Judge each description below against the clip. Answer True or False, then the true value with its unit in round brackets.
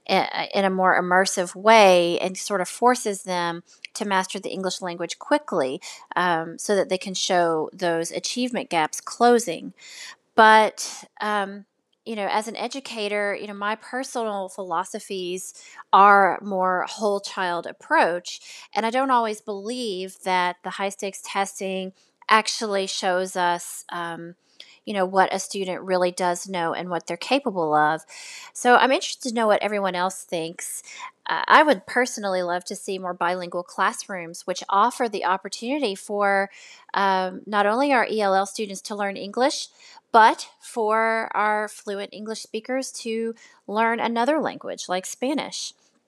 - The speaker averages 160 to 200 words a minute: False (150 wpm)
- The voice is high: True (200 Hz)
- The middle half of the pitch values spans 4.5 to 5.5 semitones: False (3.3 semitones)